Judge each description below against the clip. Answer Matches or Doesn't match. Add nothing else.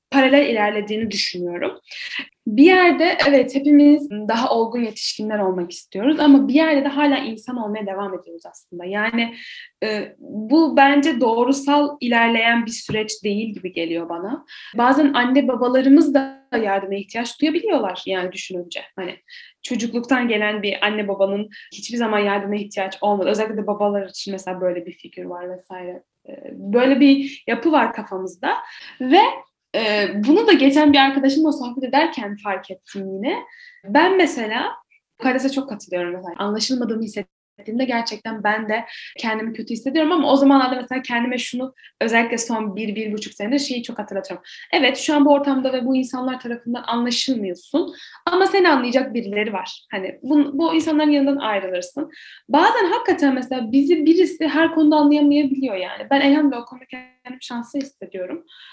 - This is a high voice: Matches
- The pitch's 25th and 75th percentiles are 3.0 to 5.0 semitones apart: Doesn't match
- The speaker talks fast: Matches